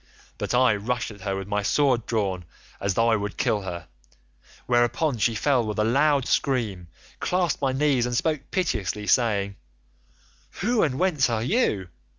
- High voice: No, low, 120 Hz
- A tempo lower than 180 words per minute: Yes, average, 165 wpm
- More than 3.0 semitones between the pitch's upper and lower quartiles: Yes, average, 5.2 semitones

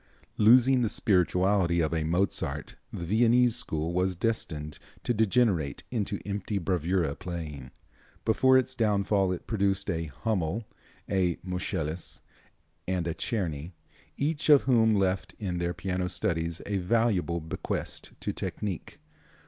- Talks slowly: Yes, slow, 130 wpm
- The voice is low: Yes, very low, 95 Hz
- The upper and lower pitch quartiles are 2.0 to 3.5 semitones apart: No, average, 4.6 semitones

